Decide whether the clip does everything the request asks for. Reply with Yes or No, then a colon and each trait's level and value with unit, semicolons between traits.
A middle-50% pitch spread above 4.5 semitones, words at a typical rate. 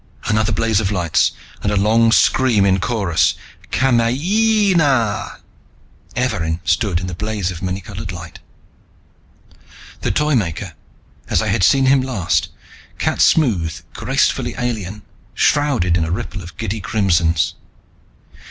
No: average, 5.3 semitones; slow, 130 wpm